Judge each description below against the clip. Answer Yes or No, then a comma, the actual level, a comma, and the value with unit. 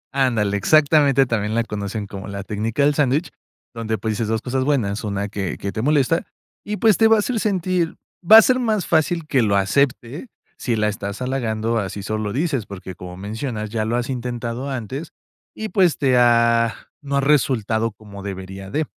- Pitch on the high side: No, low, 120 Hz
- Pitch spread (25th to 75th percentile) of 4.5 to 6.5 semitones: Yes, wide, 5.6 semitones